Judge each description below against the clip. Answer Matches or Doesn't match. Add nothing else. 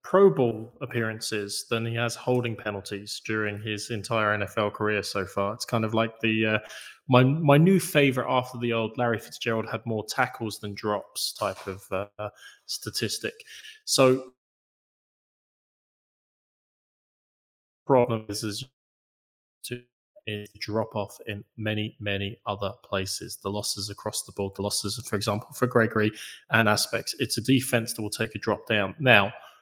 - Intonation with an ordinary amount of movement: Matches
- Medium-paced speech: Matches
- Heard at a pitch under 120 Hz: Matches